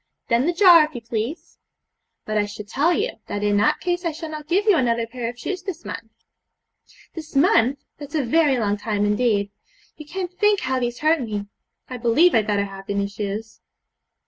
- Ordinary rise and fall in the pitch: No, wide, 7.3 semitones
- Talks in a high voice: Yes, high, 245 Hz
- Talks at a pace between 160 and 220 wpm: Yes, fast, 205 wpm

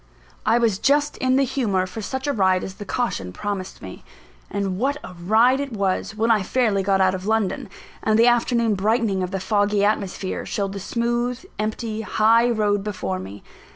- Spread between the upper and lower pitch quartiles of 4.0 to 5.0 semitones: No, average, 3.5 semitones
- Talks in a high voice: Yes, high, 215 Hz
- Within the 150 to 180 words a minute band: No, average, 190 wpm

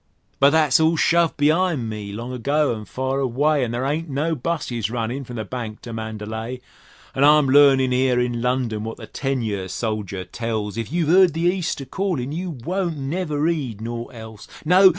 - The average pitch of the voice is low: Yes, low, 130 Hz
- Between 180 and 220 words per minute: Yes, average, 190 wpm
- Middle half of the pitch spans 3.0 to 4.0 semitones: No, average, 5.2 semitones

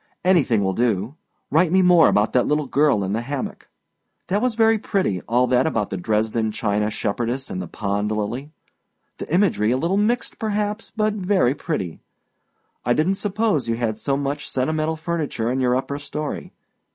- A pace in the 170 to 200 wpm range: Yes, average, 175 wpm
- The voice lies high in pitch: No, medium, 140 Hz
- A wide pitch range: Yes, wide, 8.3 semitones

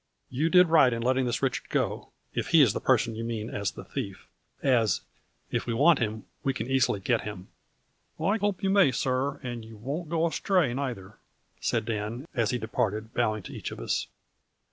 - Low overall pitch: Yes, low, 120 Hz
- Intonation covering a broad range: No, average, 4.2 semitones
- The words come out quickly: Yes, fast, 210 wpm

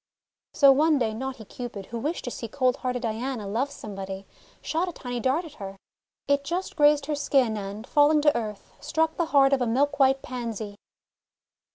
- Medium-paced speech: Yes, average, 190 wpm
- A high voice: Yes, very high, 260 Hz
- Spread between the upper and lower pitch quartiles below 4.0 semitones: No, average, 4.6 semitones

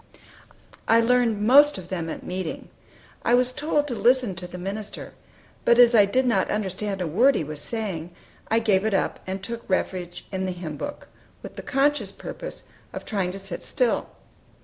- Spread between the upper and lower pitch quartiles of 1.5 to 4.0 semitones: No, average, 4.8 semitones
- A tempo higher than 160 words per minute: Yes, average, 190 wpm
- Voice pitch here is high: Yes, high, 210 Hz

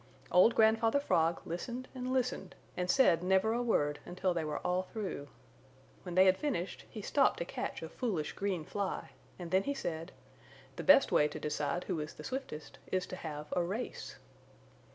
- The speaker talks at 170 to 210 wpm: Yes, average, 185 wpm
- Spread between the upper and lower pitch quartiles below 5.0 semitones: No, wide, 5.5 semitones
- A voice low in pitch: No, medium, 185 Hz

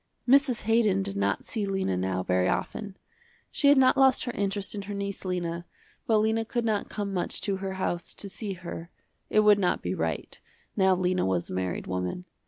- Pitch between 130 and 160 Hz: No, high, 195 Hz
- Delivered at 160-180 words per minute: No, average, 200 wpm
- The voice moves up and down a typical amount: Yes, average, 3.7 semitones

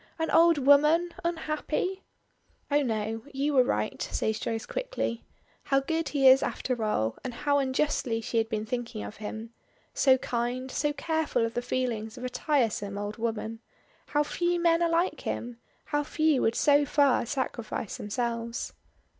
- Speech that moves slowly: No, average, 165 wpm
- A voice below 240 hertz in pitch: No, very high, 255 Hz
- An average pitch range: Yes, average, 4.8 semitones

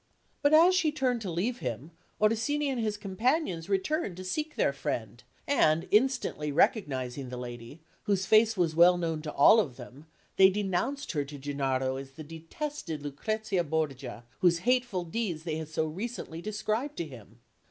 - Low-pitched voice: No, medium, 175 Hz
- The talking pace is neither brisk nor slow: Yes, average, 170 wpm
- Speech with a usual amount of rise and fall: No, wide, 7.3 semitones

